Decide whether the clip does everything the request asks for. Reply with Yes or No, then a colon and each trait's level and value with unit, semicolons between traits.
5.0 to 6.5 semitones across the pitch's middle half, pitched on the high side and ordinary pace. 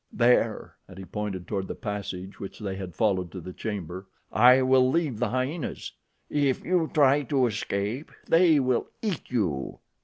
No: wide, 5.5 semitones; low, 115 Hz; average, 165 wpm